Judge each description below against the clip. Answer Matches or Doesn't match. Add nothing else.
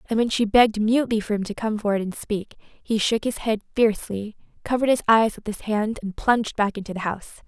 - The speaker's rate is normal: Doesn't match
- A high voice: Matches